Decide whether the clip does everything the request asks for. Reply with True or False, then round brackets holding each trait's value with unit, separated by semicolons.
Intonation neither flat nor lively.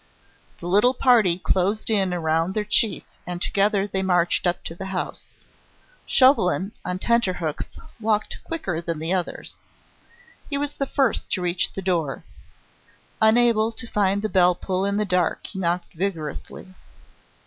True (3.4 semitones)